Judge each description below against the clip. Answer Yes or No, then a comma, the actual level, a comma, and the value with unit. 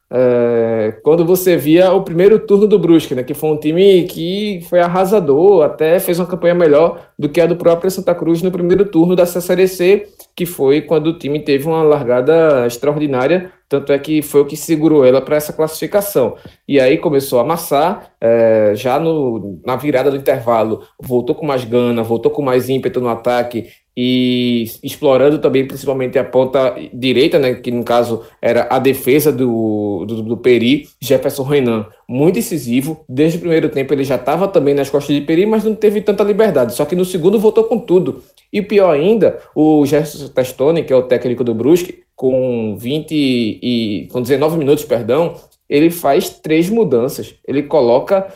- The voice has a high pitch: No, medium, 150 Hz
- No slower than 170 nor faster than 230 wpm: Yes, average, 180 wpm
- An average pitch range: No, wide, 5.9 semitones